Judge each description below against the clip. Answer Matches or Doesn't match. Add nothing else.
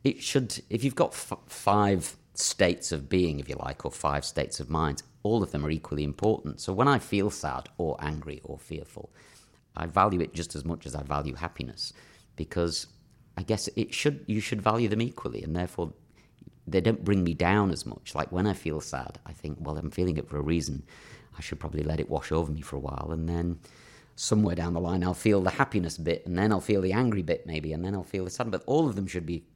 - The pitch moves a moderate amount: Matches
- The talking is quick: Matches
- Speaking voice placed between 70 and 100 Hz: Matches